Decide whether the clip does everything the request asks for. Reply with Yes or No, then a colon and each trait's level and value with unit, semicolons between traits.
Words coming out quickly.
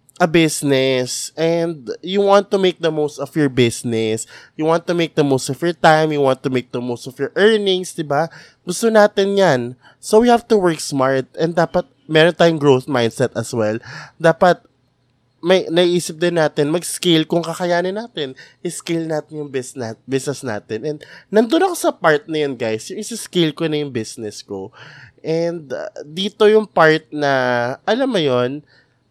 Yes: fast, 175 wpm